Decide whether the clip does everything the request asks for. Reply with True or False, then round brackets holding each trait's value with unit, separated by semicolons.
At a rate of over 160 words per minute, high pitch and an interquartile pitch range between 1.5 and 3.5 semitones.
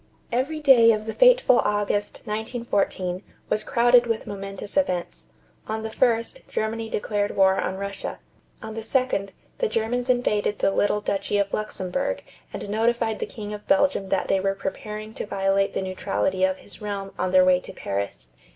True (170 wpm; 210 Hz; 3.0 semitones)